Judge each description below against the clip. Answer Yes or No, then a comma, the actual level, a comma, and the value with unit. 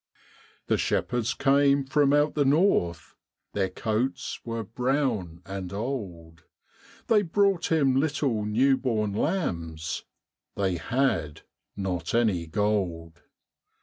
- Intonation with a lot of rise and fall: Yes, wide, 7.3 semitones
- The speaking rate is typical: No, slow, 110 wpm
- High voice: No, low, 115 Hz